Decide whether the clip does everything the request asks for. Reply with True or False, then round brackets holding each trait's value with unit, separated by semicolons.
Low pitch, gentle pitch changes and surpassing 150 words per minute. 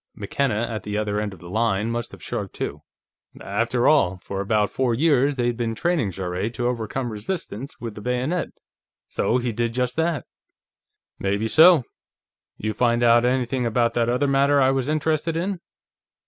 False (120 Hz; 4.1 semitones; 175 wpm)